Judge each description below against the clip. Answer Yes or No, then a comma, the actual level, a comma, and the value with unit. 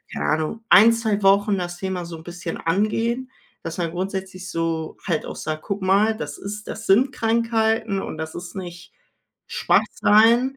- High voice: Yes, high, 195 Hz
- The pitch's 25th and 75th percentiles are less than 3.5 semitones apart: No, average, 4.2 semitones